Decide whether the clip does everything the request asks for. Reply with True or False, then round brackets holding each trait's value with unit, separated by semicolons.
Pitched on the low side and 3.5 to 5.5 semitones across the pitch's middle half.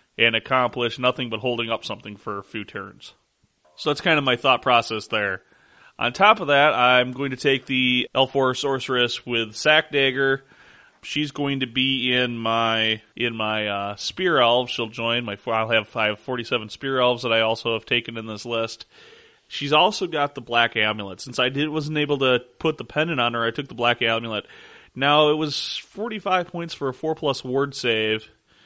True (125 Hz; 4.0 semitones)